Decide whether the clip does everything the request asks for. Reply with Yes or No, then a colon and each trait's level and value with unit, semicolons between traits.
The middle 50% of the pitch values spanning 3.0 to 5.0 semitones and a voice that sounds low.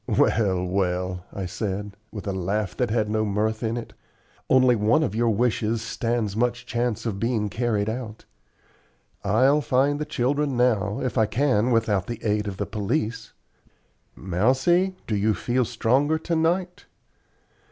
Yes: average, 3.5 semitones; low, 115 Hz